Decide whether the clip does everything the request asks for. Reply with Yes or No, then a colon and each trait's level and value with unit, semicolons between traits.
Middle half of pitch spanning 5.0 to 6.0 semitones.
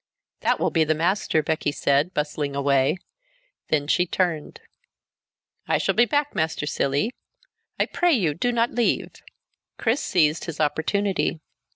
Yes: wide, 5.6 semitones